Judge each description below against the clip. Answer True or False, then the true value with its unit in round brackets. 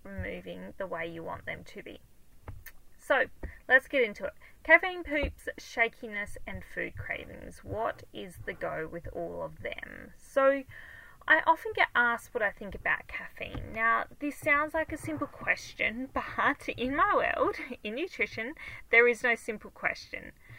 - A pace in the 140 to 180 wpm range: True (160 wpm)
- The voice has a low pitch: False (265 Hz)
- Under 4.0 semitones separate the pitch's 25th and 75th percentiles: False (4.9 semitones)